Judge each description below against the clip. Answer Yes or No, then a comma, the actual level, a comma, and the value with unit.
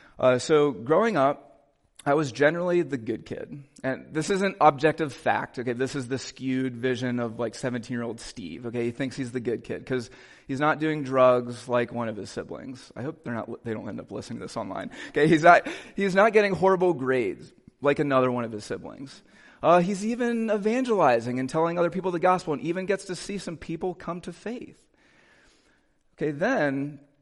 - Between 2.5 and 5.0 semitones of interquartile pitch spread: No, wide, 5.5 semitones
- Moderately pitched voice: Yes, medium, 145 Hz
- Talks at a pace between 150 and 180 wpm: No, fast, 205 wpm